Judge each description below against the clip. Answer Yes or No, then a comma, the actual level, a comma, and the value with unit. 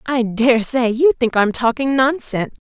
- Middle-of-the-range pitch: No, high, 245 Hz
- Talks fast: No, average, 180 wpm